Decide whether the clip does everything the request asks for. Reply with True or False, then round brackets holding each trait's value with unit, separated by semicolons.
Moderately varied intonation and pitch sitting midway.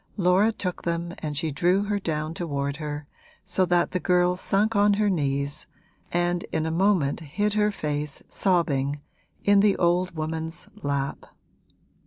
True (4.1 semitones; 175 Hz)